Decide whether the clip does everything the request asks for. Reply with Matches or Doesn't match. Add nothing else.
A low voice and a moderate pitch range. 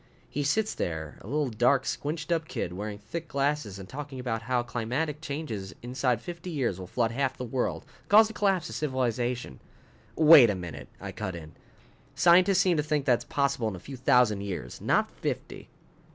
Doesn't match